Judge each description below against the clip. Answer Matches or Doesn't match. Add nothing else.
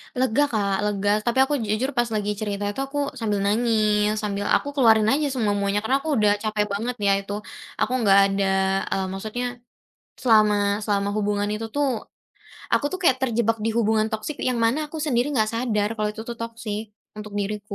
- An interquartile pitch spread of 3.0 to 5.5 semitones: Doesn't match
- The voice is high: Matches